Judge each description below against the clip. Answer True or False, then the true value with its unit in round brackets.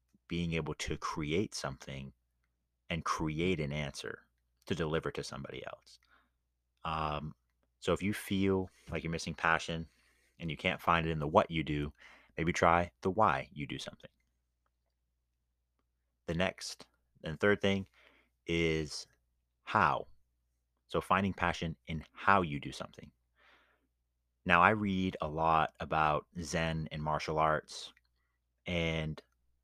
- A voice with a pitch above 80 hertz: False (75 Hz)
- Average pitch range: False (5.7 semitones)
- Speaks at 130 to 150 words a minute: True (135 wpm)